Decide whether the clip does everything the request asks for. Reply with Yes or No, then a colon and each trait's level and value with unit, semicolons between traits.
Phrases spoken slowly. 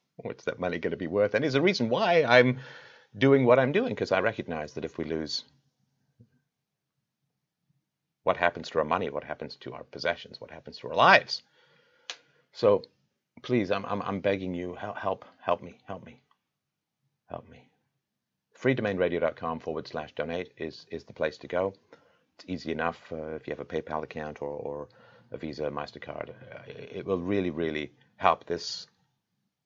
No: average, 175 wpm